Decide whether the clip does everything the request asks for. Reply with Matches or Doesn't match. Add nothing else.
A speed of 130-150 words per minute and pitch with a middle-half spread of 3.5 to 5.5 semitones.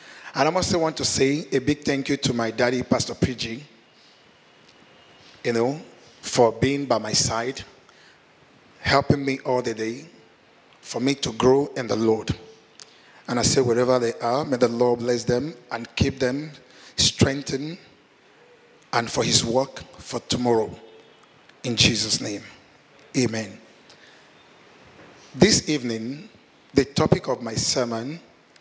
Doesn't match